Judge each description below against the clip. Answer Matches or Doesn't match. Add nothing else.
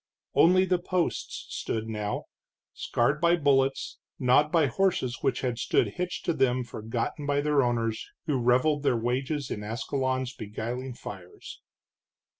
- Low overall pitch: Matches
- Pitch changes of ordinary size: Matches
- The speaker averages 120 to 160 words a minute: Matches